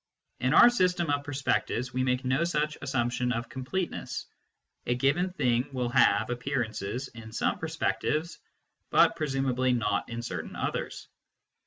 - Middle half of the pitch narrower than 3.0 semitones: No, average, 3.3 semitones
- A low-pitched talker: Yes, low, 130 Hz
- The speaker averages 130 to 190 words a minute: Yes, average, 140 wpm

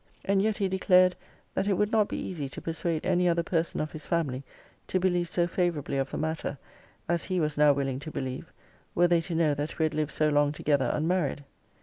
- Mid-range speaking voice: Yes, medium, 165 Hz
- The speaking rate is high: Yes, fast, 225 wpm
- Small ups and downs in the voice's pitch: No, average, 3.5 semitones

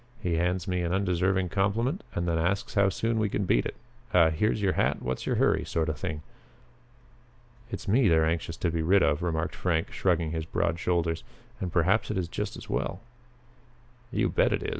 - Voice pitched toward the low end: Yes, very low, 90 Hz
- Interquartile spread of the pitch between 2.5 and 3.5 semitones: Yes, average, 3.1 semitones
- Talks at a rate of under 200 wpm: No, fast, 205 wpm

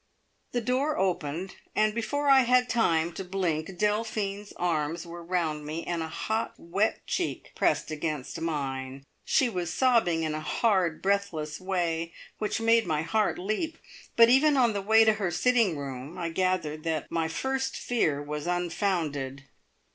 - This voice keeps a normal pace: Yes, average, 160 wpm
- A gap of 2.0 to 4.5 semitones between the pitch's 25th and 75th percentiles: No, wide, 5.5 semitones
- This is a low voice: No, medium, 180 Hz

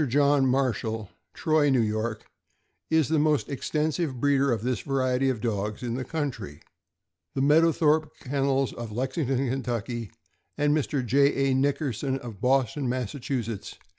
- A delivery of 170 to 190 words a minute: No, average, 145 wpm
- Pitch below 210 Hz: Yes, low, 135 Hz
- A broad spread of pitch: No, average, 3.2 semitones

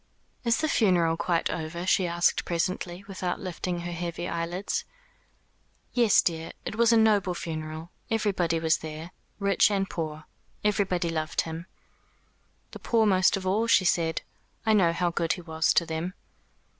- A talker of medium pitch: Yes, medium, 175 Hz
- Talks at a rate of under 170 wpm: Yes, average, 155 wpm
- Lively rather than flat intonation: No, average, 3.0 semitones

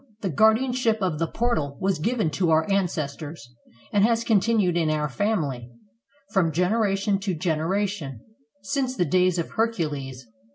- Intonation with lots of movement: Yes, wide, 5.8 semitones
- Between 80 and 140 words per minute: No, average, 150 wpm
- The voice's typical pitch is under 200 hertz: Yes, medium, 185 Hz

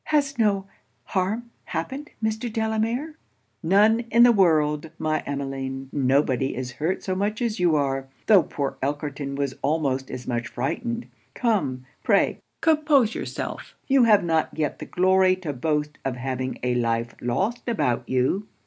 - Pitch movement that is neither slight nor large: No, wide, 8.4 semitones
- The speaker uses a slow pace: No, average, 150 wpm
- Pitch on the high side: No, medium, 160 Hz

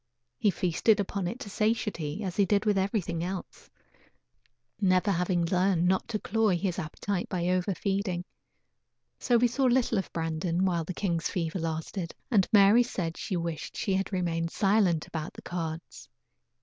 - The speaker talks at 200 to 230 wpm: No, average, 165 wpm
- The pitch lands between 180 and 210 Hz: Yes, medium, 185 Hz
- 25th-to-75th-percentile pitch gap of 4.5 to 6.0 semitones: No, average, 3.2 semitones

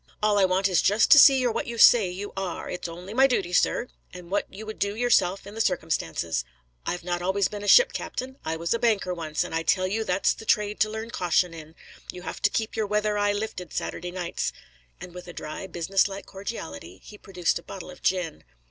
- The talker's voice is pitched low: No, high, 195 Hz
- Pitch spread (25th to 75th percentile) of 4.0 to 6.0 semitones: No, average, 3.2 semitones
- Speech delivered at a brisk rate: Yes, fast, 235 wpm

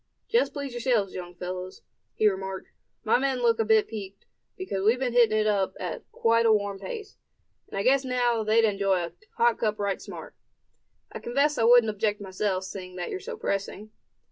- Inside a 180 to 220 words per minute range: Yes, average, 195 wpm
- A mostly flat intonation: No, average, 3.7 semitones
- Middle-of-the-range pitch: No, high, 215 Hz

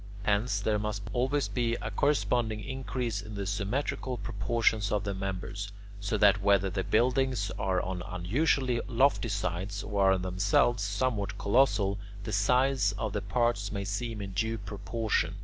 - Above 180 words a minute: No, average, 155 wpm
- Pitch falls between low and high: No, low, 105 Hz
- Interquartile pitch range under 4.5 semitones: Yes, average, 3.3 semitones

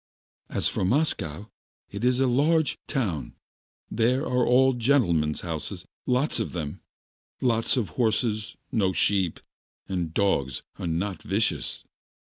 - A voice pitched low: Yes, low, 110 Hz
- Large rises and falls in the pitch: Yes, wide, 6.3 semitones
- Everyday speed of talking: No, slow, 115 wpm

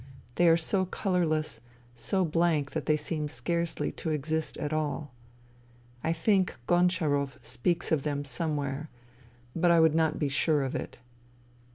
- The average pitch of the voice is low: No, medium, 155 Hz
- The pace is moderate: Yes, average, 150 wpm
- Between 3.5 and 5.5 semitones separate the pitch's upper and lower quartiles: No, average, 2.8 semitones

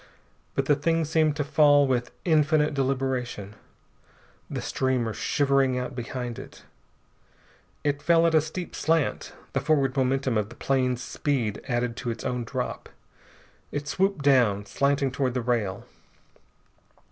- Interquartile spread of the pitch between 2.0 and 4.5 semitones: Yes, average, 3.0 semitones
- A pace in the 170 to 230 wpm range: No, average, 140 wpm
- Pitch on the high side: No, low, 135 Hz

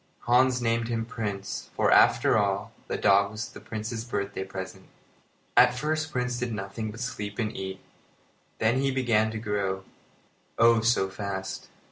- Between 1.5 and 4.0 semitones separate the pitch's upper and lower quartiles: Yes, average, 3.3 semitones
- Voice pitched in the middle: No, low, 110 Hz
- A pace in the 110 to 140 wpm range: No, average, 155 wpm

